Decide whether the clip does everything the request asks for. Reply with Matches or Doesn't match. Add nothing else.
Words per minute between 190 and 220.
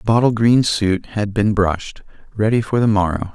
Matches